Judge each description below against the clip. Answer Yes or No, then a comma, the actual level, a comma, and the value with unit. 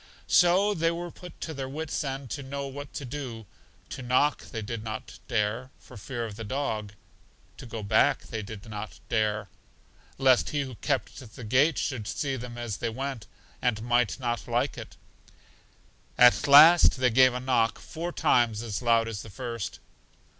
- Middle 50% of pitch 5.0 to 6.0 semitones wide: No, average, 3.8 semitones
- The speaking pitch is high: No, low, 125 Hz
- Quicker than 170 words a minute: Yes, average, 180 wpm